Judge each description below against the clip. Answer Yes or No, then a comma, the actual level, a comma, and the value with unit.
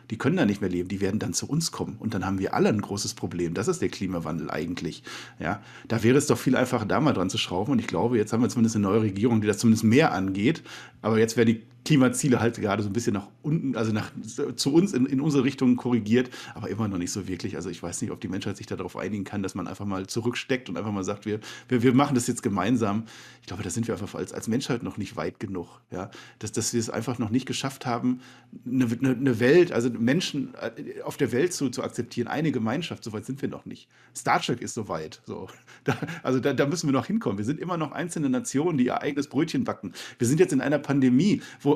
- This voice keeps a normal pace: No, fast, 260 wpm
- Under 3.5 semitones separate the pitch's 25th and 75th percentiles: No, average, 3.8 semitones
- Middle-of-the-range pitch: No, low, 120 Hz